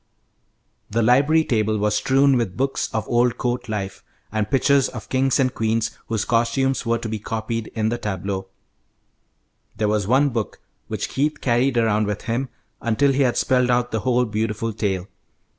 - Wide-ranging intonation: No, average, 3.1 semitones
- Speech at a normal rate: Yes, average, 175 wpm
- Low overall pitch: Yes, low, 115 Hz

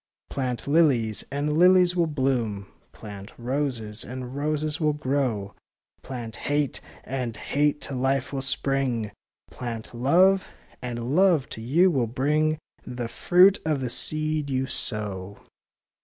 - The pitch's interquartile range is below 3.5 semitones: No, average, 4.3 semitones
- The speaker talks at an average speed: No, slow, 130 wpm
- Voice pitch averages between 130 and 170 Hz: Yes, low, 135 Hz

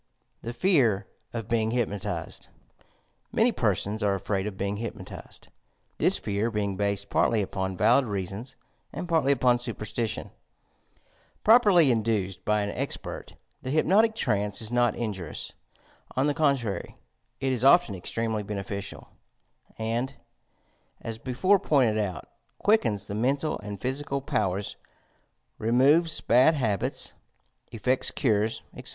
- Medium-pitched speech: No, low, 115 Hz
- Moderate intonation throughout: Yes, average, 4.6 semitones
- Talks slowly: Yes, slow, 125 wpm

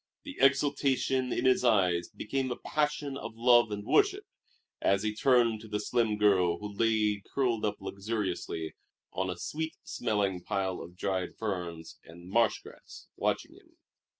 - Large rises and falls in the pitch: No, average, 4.5 semitones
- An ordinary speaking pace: Yes, average, 155 wpm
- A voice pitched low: Yes, low, 105 Hz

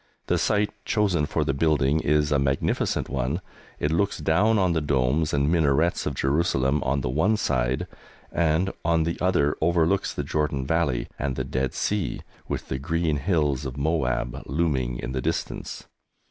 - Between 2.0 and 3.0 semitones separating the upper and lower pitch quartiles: No, average, 3.8 semitones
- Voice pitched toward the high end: No, very low, 75 Hz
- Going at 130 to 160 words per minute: No, average, 170 wpm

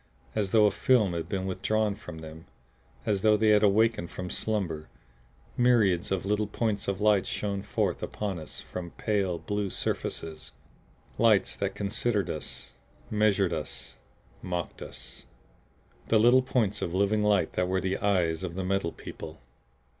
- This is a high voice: No, low, 100 Hz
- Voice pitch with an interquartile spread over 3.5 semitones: No, average, 2.9 semitones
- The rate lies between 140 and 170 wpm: Yes, average, 160 wpm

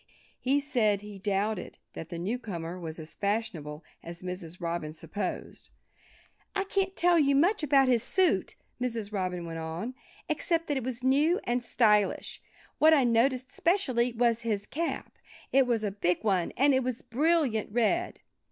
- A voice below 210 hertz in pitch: No, high, 230 Hz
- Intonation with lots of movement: Yes, wide, 6.2 semitones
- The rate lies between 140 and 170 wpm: Yes, average, 165 wpm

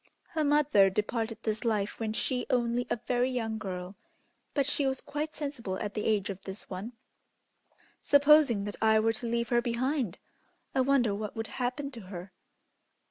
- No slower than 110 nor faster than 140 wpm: No, average, 175 wpm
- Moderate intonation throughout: Yes, average, 4.1 semitones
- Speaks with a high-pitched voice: Yes, high, 235 Hz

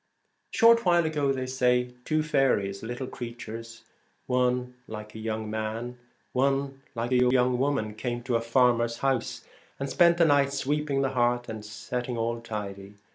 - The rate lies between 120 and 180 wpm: No, average, 190 wpm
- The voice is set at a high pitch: No, low, 125 Hz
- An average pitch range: Yes, average, 3.0 semitones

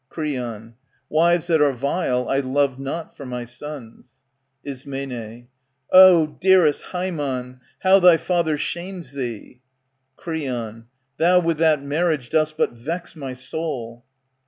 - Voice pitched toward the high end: No, medium, 145 Hz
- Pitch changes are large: No, average, 4.7 semitones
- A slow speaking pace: Yes, slow, 125 wpm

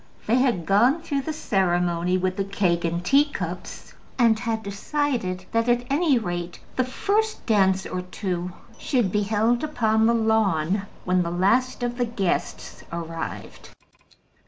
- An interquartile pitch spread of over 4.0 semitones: Yes, average, 5.1 semitones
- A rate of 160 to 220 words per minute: No, average, 150 wpm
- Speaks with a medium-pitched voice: No, high, 210 Hz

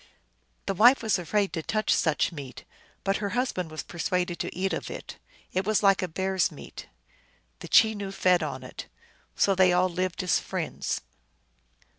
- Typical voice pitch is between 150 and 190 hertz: Yes, medium, 185 Hz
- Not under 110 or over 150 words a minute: No, average, 175 wpm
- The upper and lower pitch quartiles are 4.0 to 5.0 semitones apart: No, narrow, 2.4 semitones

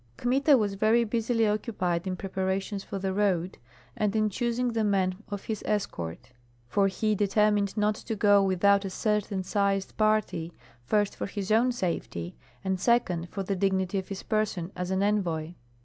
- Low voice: No, high, 200 Hz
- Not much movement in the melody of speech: Yes, narrow, 2.2 semitones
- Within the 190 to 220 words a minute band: No, average, 170 wpm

